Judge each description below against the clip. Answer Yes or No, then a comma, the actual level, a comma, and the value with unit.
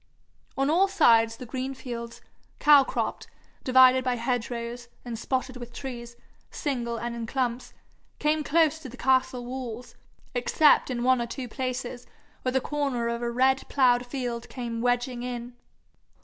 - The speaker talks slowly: No, average, 160 wpm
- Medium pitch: No, very high, 250 Hz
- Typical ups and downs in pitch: No, narrow, 1.8 semitones